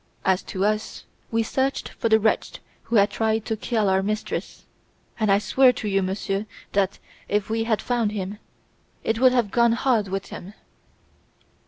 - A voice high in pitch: Yes, high, 215 Hz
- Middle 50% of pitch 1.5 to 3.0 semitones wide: Yes, narrow, 2.4 semitones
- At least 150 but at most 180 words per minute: Yes, average, 175 wpm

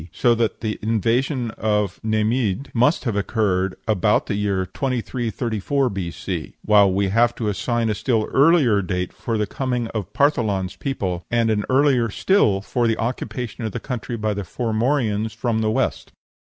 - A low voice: Yes, low, 110 Hz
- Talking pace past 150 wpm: Yes, average, 170 wpm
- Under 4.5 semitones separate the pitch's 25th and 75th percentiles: Yes, average, 3.1 semitones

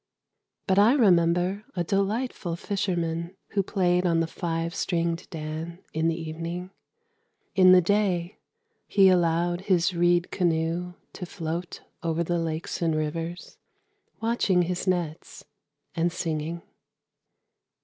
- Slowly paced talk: Yes, slow, 120 wpm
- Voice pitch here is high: No, medium, 175 Hz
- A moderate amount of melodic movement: No, narrow, 1.8 semitones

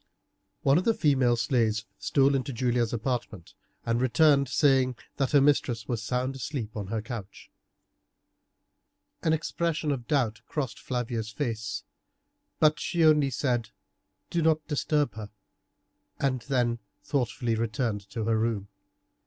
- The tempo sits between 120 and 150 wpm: Yes, slow, 135 wpm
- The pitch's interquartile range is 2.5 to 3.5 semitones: No, average, 3.9 semitones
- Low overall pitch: Yes, low, 125 Hz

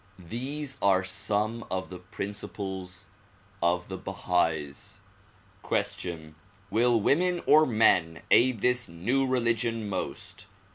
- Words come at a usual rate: No, slow, 105 wpm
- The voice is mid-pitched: No, low, 100 Hz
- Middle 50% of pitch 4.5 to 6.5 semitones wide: Yes, average, 5.3 semitones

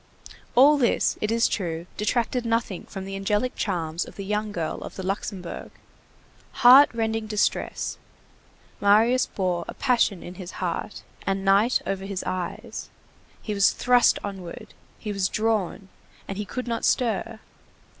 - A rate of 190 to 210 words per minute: No, average, 150 wpm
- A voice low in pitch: No, high, 205 Hz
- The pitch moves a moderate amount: Yes, average, 3.3 semitones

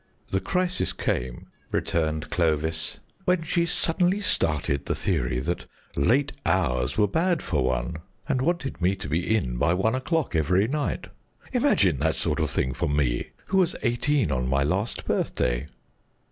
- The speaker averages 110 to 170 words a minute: Yes, average, 160 wpm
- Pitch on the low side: Yes, very low, 90 Hz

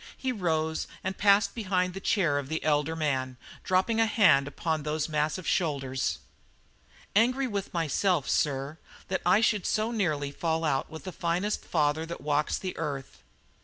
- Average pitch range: Yes, average, 4.6 semitones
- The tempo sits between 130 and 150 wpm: No, average, 165 wpm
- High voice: No, medium, 165 Hz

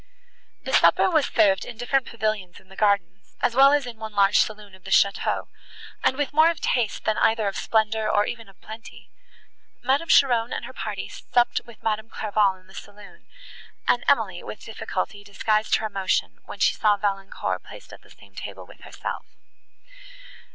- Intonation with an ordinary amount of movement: Yes, average, 3.1 semitones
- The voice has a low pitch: No, high, 215 Hz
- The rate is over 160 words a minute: Yes, average, 185 wpm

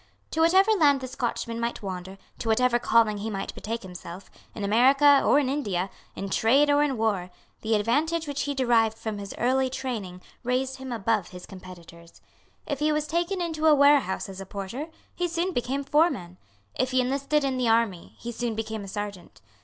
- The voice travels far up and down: Yes, wide, 5.8 semitones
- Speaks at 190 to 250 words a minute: Yes, average, 195 wpm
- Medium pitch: No, high, 240 Hz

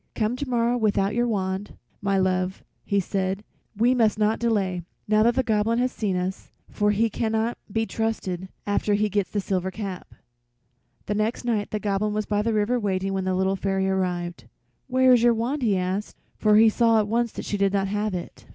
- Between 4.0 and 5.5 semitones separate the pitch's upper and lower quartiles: No, average, 2.8 semitones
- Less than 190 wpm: No, average, 200 wpm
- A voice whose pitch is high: Yes, high, 210 Hz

